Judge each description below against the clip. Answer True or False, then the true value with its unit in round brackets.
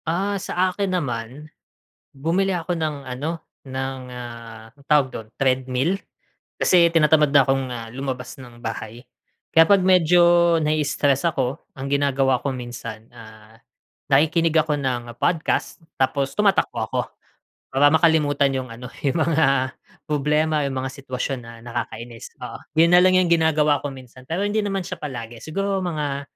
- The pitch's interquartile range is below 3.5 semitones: False (4.2 semitones)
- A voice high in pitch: False (140 Hz)